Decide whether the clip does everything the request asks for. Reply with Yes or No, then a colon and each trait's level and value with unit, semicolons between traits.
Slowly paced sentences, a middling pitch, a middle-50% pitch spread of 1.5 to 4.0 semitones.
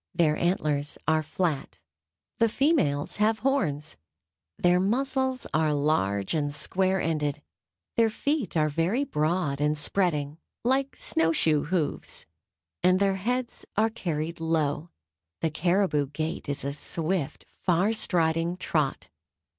No: slow, 125 wpm; medium, 165 Hz; average, 4.7 semitones